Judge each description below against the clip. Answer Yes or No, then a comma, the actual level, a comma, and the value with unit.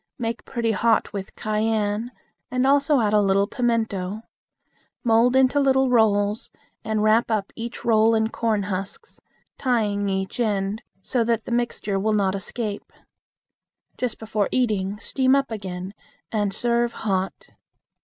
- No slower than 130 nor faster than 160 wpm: Yes, average, 140 wpm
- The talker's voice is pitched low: No, high, 220 Hz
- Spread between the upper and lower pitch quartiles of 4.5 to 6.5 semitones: No, average, 2.8 semitones